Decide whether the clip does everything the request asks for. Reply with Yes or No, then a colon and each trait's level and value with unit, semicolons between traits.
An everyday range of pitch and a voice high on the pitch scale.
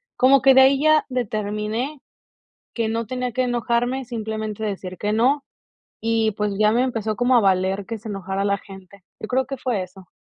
Yes: average, 3.7 semitones; high, 225 Hz